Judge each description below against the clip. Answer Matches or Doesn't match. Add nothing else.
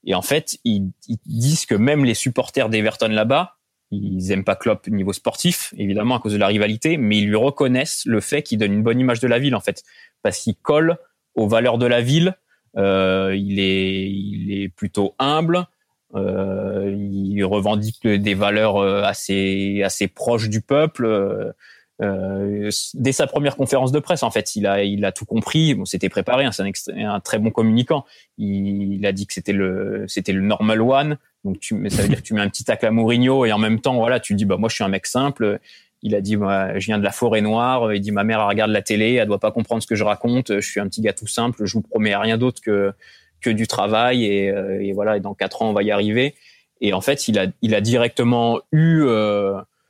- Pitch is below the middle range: Matches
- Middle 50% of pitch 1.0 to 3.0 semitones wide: Doesn't match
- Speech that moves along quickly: Matches